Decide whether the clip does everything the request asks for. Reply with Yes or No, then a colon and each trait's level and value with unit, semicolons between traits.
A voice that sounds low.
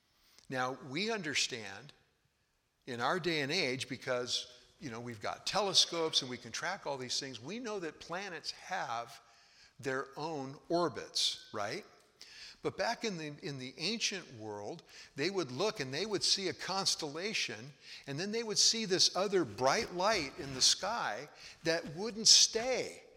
No: medium, 150 Hz